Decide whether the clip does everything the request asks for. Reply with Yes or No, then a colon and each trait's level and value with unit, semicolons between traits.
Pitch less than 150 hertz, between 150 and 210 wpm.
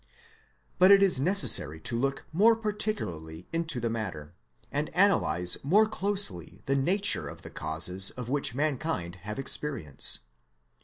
No: low, 135 Hz; average, 140 wpm